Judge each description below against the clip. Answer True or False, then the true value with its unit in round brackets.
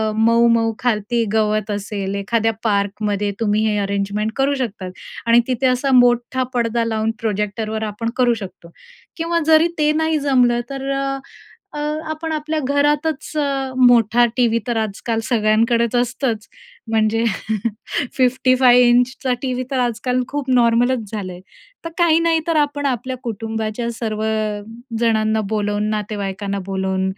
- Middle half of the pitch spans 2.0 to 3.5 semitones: True (3.2 semitones)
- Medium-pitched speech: False (230 Hz)